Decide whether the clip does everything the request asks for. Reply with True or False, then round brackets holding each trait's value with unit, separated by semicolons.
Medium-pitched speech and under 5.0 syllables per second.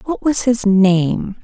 False (215 Hz; 3.2 syllables/s)